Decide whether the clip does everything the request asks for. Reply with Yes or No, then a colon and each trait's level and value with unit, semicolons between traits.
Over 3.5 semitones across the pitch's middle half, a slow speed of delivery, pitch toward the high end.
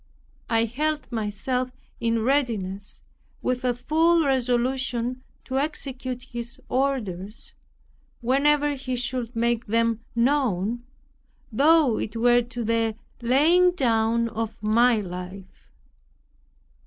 No: average, 2.8 semitones; slow, 105 wpm; high, 240 Hz